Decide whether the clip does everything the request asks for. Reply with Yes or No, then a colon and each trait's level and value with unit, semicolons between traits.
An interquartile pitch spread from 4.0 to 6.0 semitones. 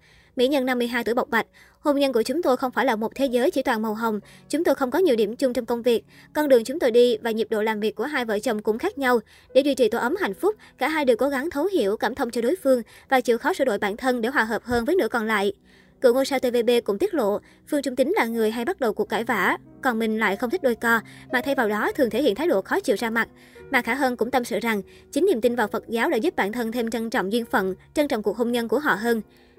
No: average, 3.0 semitones